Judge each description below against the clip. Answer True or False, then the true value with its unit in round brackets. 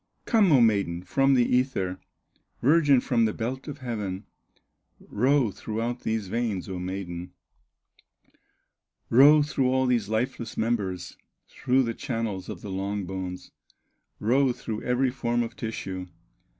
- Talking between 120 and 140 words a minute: True (135 wpm)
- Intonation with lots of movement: False (4.9 semitones)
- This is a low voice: True (115 Hz)